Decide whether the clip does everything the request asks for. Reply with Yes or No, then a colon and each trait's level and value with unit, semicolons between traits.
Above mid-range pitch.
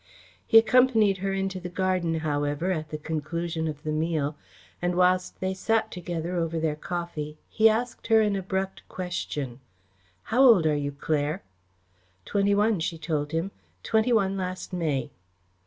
No: medium, 175 Hz